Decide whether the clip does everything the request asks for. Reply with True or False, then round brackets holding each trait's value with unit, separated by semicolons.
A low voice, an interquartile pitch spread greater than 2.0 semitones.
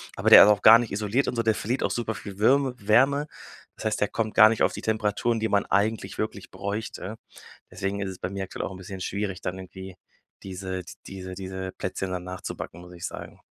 True (100 Hz; 2.7 semitones)